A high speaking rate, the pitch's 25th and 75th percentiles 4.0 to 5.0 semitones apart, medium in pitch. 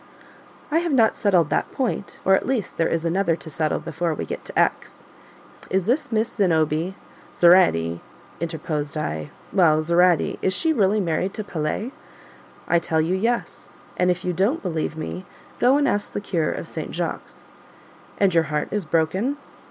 No: average, 175 wpm; average, 4.4 semitones; medium, 180 Hz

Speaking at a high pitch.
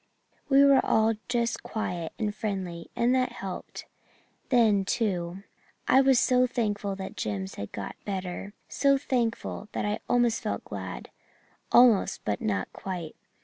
Yes: high, 210 Hz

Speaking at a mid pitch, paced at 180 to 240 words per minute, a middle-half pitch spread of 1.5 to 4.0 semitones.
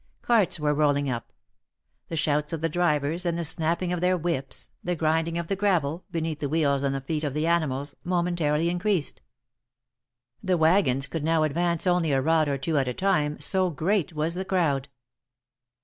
Yes: medium, 160 Hz; average, 185 wpm; average, 3.0 semitones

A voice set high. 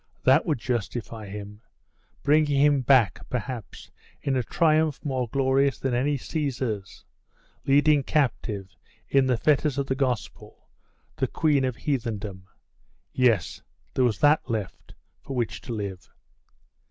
No: low, 130 Hz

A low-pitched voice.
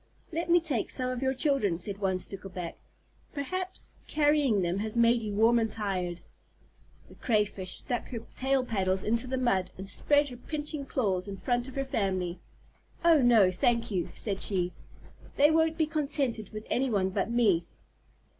No: high, 230 Hz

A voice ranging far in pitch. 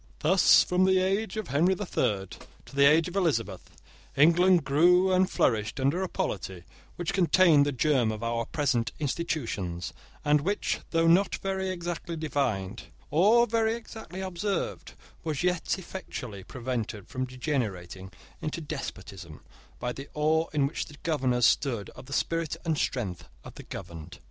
Yes: wide, 7.2 semitones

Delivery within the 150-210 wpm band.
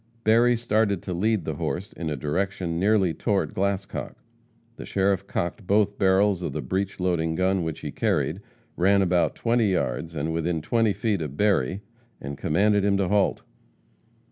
Yes: average, 170 wpm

